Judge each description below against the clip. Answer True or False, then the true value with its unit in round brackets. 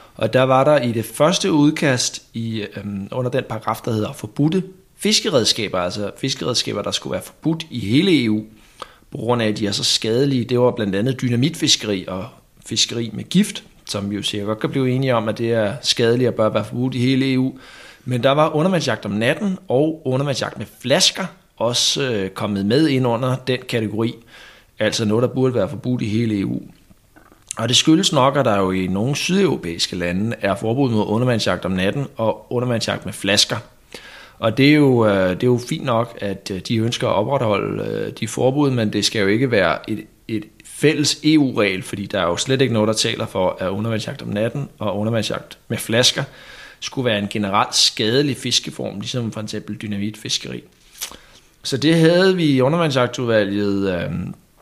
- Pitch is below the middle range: True (115 Hz)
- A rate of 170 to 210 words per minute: True (185 wpm)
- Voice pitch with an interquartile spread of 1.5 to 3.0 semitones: False (4.5 semitones)